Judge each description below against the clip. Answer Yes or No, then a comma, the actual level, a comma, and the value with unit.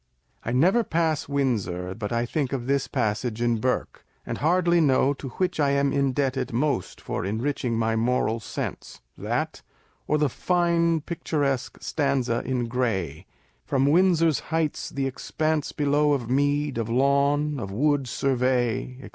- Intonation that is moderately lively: Yes, average, 3.9 semitones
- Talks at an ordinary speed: Yes, average, 150 wpm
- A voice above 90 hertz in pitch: Yes, low, 135 Hz